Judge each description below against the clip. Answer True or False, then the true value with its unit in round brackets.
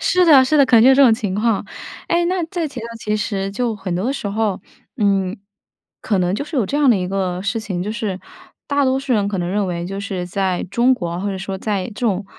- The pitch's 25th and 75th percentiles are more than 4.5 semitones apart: True (5.1 semitones)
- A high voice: True (210 Hz)